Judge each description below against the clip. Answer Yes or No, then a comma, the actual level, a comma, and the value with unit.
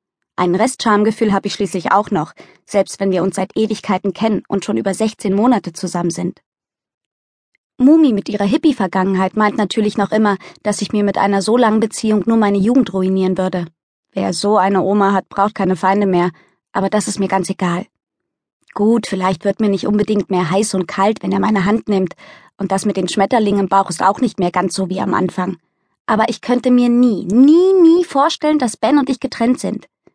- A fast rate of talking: Yes, fast, 205 wpm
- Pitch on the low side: No, high, 200 Hz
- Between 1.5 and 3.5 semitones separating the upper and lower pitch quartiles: Yes, average, 2.7 semitones